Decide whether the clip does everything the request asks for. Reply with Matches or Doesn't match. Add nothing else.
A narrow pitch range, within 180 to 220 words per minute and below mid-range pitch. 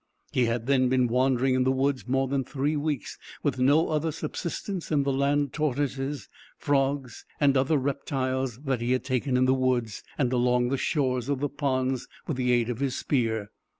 Matches